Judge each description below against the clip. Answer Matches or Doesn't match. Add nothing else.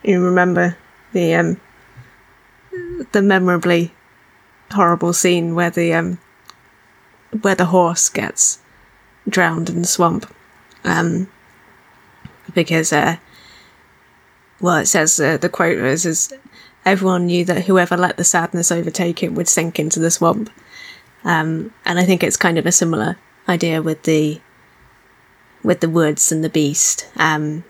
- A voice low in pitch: Doesn't match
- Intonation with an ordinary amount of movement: Doesn't match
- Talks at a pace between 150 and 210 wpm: Doesn't match